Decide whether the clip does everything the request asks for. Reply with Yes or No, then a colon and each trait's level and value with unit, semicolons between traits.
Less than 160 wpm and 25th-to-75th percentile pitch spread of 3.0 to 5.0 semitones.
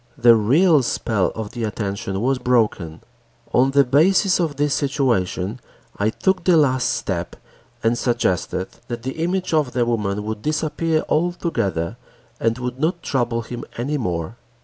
No: average, 150 wpm; wide, 5.5 semitones